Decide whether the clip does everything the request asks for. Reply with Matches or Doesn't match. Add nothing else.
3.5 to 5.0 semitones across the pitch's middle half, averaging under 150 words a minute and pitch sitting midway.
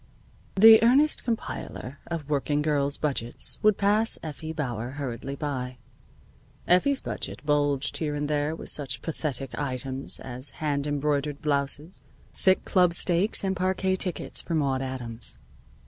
Matches